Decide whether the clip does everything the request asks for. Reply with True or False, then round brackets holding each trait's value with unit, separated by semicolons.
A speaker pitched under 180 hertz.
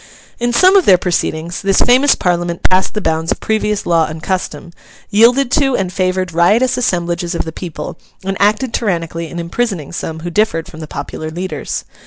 False (185 Hz)